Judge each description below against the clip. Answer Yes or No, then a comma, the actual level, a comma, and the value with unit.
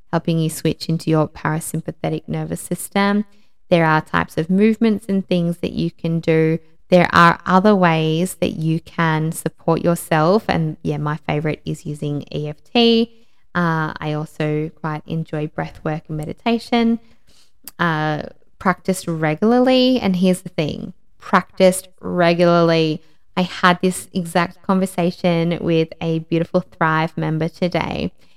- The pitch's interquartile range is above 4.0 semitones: No, average, 2.9 semitones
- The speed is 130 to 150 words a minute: Yes, slow, 135 wpm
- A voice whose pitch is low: No, medium, 170 Hz